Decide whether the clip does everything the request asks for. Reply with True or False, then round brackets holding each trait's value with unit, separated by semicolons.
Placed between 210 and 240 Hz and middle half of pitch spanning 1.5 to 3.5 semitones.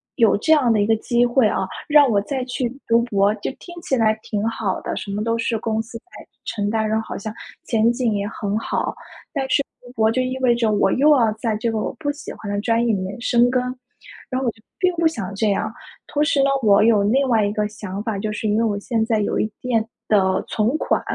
True (225 Hz; 2.8 semitones)